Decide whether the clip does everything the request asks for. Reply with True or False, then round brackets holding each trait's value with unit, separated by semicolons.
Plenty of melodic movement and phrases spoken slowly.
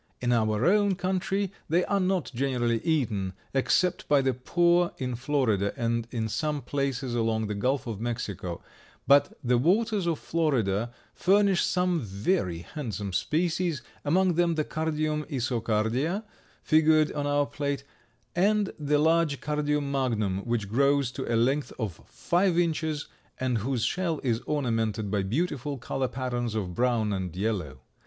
False (5.9 semitones; 150 wpm)